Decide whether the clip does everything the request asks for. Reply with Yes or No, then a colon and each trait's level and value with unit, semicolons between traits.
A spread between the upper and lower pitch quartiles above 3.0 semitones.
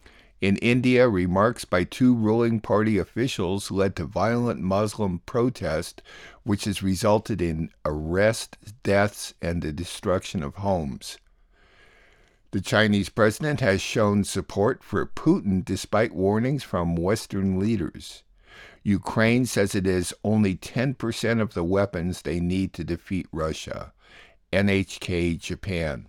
Yes: average, 3.4 semitones